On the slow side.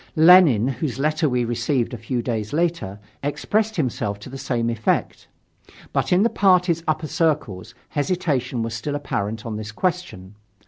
No: average, 155 wpm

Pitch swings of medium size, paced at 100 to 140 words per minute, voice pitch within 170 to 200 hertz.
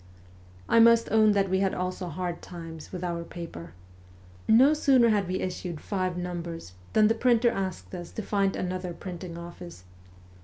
No: average, 3.6 semitones; average, 165 wpm; medium, 185 Hz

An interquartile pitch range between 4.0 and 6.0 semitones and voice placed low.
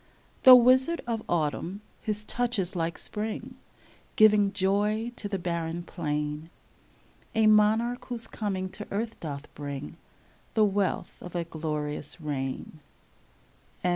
No: average, 5.1 semitones; high, 195 Hz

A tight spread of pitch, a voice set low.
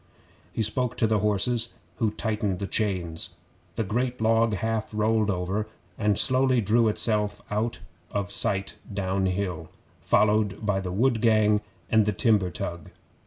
Yes: narrow, 2.3 semitones; low, 105 Hz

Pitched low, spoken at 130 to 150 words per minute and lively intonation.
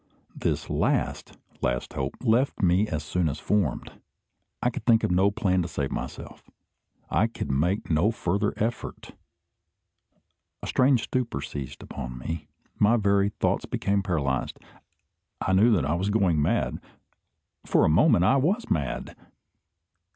Yes: very low, 95 Hz; average, 145 wpm; wide, 6.2 semitones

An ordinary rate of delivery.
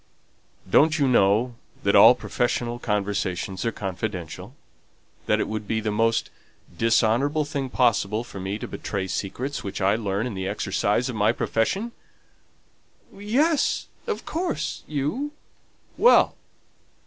No: slow, 130 wpm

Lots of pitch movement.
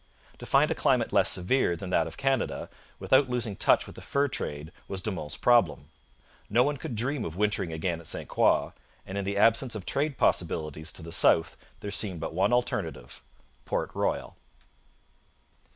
Yes: wide, 6.8 semitones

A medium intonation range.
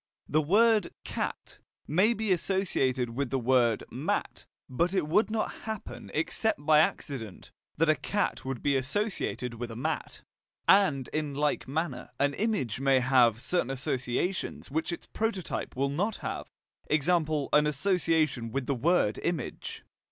No: wide, 5.7 semitones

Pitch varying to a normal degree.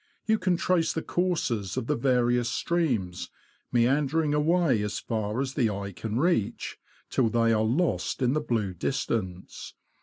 No: wide, 6.1 semitones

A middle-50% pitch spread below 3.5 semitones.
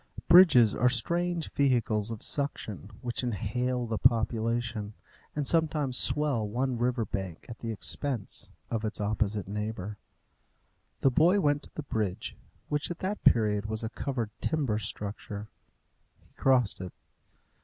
No: average, 4.6 semitones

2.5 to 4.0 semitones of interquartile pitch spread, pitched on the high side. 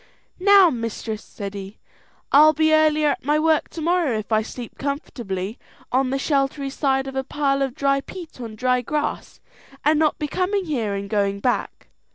No: average, 5.1 semitones; very high, 275 Hz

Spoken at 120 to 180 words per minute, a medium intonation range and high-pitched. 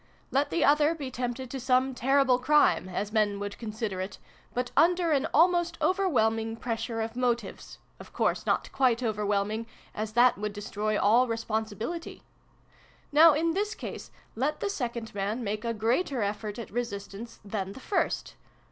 Yes: average, 160 wpm; average, 4.5 semitones; high, 235 Hz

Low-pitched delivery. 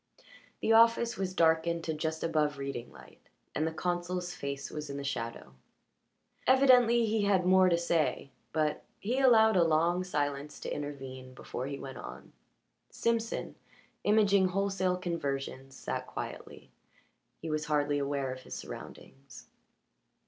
No: medium, 160 Hz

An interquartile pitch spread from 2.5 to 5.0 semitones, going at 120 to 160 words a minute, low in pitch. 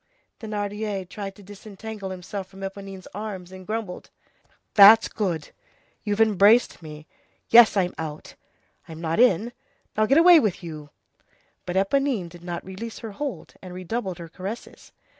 No: average, 3.4 semitones; average, 145 wpm; high, 195 Hz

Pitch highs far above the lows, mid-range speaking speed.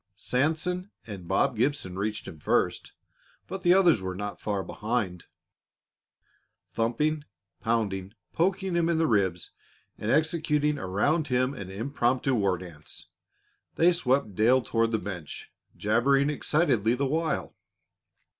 No: wide, 7.2 semitones; slow, 125 wpm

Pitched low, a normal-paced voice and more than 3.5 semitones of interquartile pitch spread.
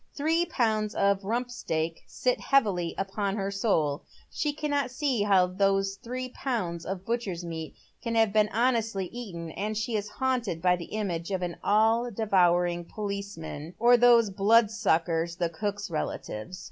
No: high, 200 Hz; average, 160 wpm; average, 4.7 semitones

